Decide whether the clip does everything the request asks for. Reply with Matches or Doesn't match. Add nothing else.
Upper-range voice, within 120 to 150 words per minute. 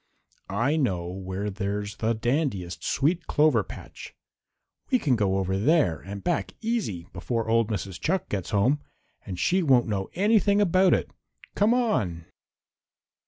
Doesn't match